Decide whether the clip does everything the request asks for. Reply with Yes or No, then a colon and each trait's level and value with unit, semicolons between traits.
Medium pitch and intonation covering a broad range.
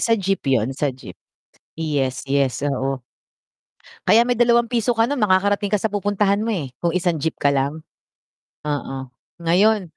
Yes: medium, 175 Hz; wide, 7.3 semitones